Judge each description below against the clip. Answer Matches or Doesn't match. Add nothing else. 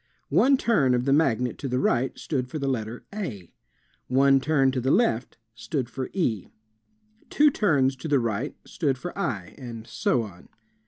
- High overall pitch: Doesn't match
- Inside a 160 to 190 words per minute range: Matches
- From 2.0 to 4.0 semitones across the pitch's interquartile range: Matches